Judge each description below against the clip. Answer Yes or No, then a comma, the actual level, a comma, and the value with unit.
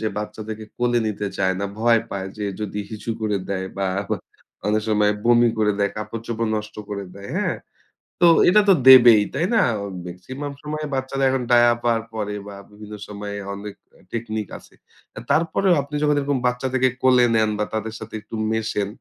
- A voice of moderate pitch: No, low, 110 Hz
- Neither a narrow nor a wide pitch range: Yes, average, 3.6 semitones